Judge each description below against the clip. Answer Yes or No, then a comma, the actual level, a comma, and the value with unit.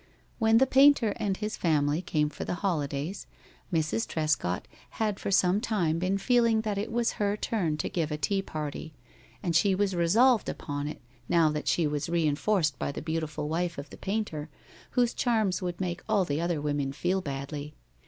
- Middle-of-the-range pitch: Yes, medium, 175 Hz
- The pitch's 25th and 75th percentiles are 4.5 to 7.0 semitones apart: Yes, wide, 5.4 semitones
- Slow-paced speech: No, average, 185 wpm